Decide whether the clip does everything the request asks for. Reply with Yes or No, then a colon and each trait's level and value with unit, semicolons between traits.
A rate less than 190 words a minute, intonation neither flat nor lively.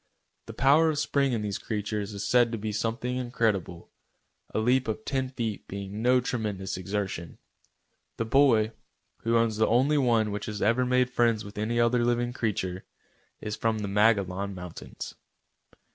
Yes: average, 165 wpm; average, 3.1 semitones